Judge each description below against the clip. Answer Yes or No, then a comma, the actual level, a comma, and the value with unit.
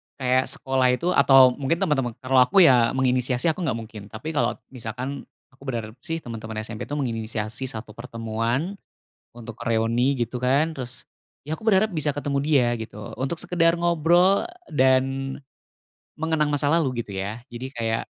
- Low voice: Yes, low, 130 Hz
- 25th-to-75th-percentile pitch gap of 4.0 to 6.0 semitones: Yes, average, 4.3 semitones